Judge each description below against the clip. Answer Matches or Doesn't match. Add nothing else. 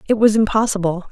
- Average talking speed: Matches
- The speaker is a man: Doesn't match